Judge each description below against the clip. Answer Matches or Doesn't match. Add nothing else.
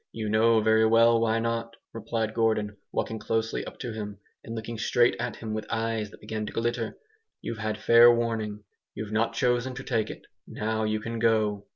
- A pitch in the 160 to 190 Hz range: Doesn't match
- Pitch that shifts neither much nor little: Doesn't match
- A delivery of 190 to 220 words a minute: Matches